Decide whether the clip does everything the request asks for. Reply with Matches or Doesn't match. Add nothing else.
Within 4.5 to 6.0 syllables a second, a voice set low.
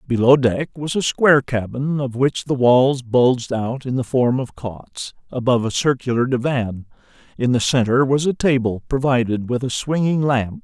Matches